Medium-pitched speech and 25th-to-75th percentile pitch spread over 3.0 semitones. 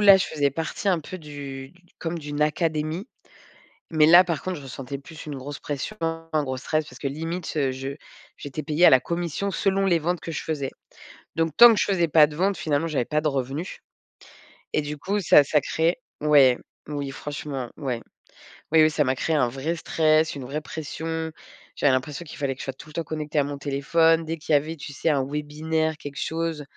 No: medium, 155 Hz; narrow, 2.5 semitones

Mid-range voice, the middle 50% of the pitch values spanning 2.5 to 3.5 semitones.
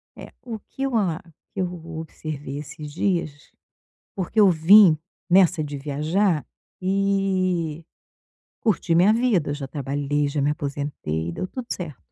No: medium, 165 Hz; average, 4.9 semitones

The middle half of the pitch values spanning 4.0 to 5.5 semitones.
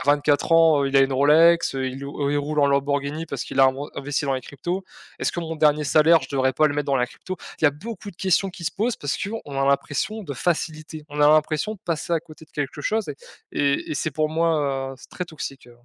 No: average, 2.9 semitones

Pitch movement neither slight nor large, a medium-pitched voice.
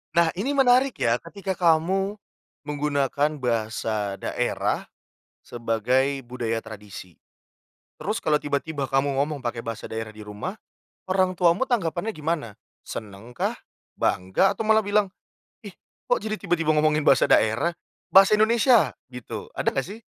No: wide, 8.8 semitones; medium, 150 Hz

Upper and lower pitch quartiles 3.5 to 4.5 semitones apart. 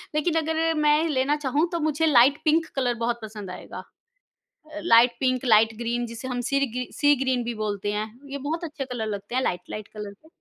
No: average, 4.9 semitones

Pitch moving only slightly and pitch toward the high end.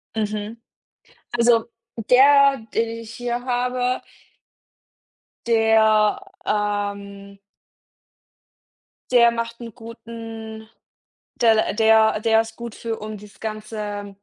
Yes: narrow, 1.7 semitones; high, 225 Hz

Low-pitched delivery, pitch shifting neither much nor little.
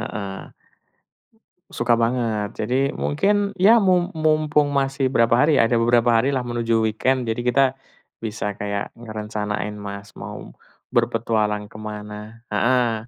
Yes: low, 115 Hz; average, 4.0 semitones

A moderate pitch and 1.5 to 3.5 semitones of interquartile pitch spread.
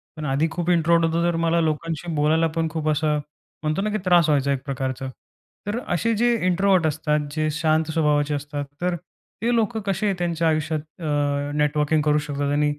Yes: medium, 155 Hz; narrow, 2.4 semitones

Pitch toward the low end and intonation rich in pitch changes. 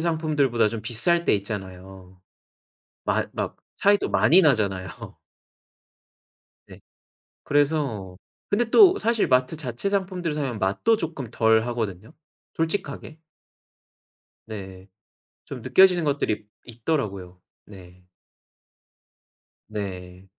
Yes: low, 120 Hz; wide, 8.8 semitones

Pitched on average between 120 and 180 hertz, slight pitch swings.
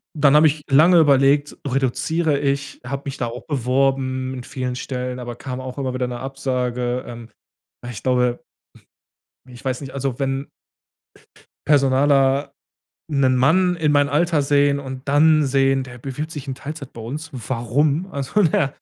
Yes: low, 135 Hz; narrow, 2.2 semitones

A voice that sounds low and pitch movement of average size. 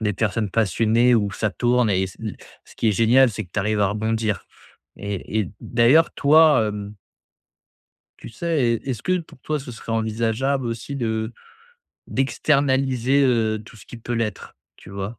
Yes: low, 115 Hz; average, 3.4 semitones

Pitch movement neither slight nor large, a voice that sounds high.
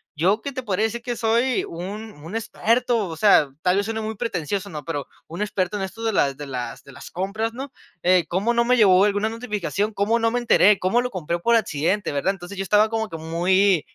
Yes: average, 4.2 semitones; high, 205 Hz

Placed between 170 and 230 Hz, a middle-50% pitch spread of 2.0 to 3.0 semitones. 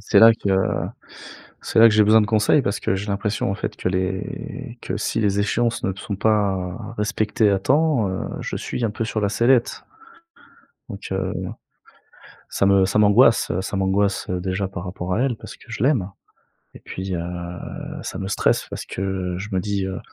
No: low, 100 Hz; narrow, 2.5 semitones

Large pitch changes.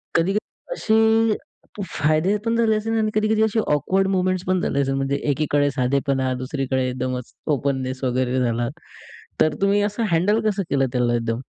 Yes: wide, 8.1 semitones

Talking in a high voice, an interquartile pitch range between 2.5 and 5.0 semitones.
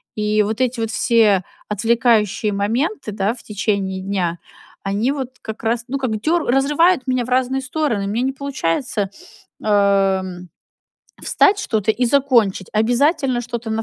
Yes: high, 225 Hz; average, 4.2 semitones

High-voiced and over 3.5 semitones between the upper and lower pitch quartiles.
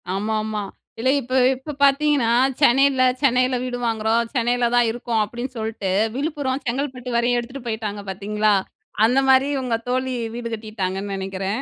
No: high, 240 Hz; average, 3.1 semitones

